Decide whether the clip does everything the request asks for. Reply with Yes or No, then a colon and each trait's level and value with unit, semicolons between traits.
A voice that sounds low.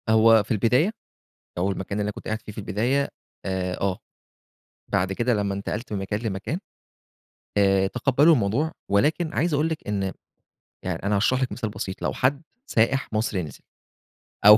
Yes: low, 105 Hz